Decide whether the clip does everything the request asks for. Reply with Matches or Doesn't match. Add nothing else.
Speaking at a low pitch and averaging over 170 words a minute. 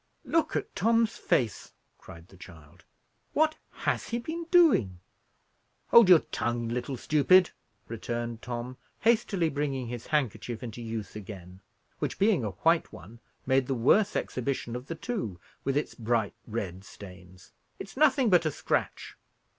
Doesn't match